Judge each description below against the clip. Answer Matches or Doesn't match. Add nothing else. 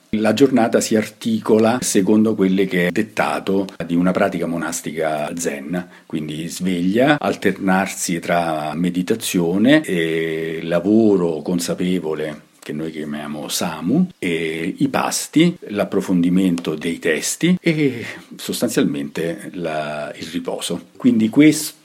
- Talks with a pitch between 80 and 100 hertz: Matches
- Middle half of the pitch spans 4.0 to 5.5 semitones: Matches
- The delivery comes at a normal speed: Doesn't match